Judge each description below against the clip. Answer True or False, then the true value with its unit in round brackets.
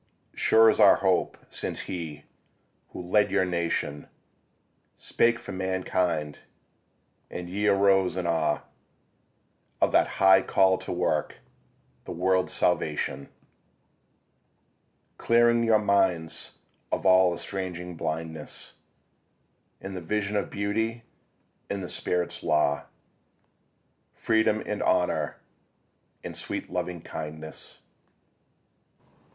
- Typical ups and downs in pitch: True (3.3 semitones)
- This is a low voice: True (95 Hz)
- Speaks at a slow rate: True (100 wpm)